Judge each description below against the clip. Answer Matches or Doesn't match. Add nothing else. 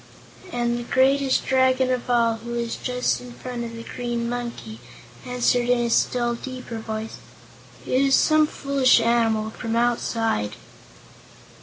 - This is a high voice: Matches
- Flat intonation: Matches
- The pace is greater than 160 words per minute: Doesn't match